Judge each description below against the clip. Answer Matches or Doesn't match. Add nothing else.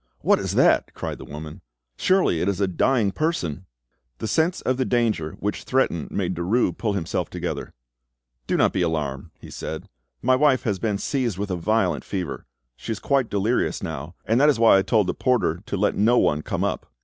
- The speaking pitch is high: Doesn't match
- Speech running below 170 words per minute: Doesn't match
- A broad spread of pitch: Matches